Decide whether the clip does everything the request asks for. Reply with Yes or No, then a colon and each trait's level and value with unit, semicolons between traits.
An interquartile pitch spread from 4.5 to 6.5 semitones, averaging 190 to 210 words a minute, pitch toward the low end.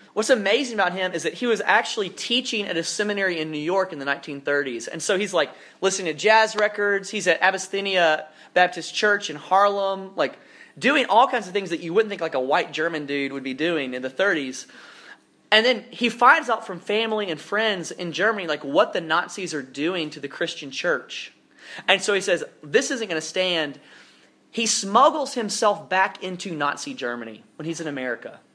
No: average, 5.2 semitones; average, 200 wpm; medium, 185 Hz